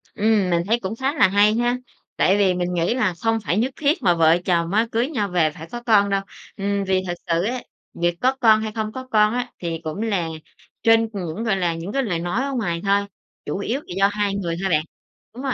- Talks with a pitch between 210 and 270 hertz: No, high, 200 Hz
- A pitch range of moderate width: Yes, average, 4.4 semitones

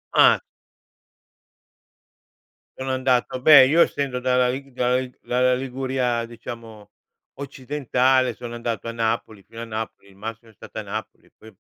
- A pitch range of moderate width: No, narrow, 2.3 semitones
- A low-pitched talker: Yes, low, 125 Hz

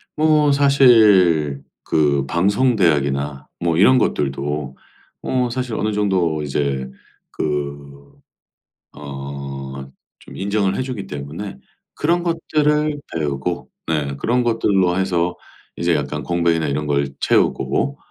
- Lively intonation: Yes, wide, 8.0 semitones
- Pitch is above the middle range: No, very low, 85 Hz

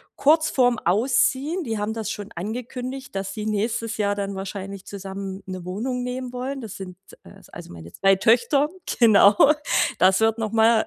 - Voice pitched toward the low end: No, high, 220 Hz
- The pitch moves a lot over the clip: No, average, 4.1 semitones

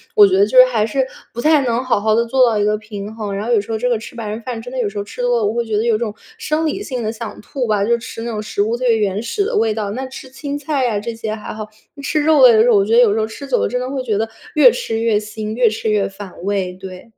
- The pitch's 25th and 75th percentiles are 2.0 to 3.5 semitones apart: Yes, average, 3.2 semitones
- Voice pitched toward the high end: Yes, high, 230 Hz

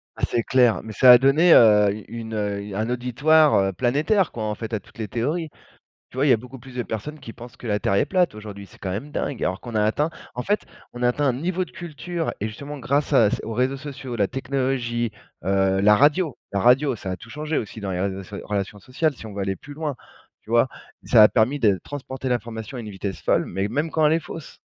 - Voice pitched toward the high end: No, low, 120 Hz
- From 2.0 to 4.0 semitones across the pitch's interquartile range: No, average, 5.3 semitones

